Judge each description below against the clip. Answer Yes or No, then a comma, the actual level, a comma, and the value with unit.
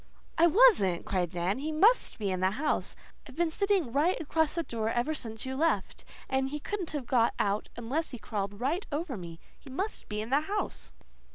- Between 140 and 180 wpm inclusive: No, fast, 205 wpm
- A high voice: Yes, very high, 270 Hz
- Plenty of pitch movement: Yes, wide, 7.1 semitones